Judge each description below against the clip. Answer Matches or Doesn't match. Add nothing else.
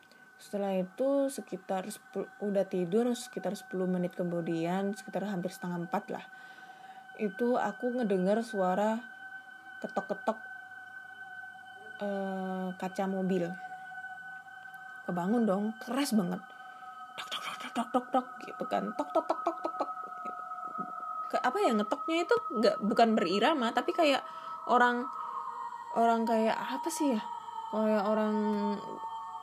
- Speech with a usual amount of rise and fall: Doesn't match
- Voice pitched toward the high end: Matches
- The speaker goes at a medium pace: Matches